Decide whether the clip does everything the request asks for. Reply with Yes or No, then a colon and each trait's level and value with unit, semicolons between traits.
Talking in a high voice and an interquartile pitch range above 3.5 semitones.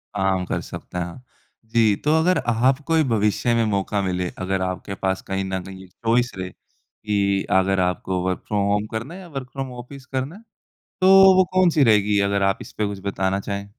No: low, 100 Hz; average, 5.0 semitones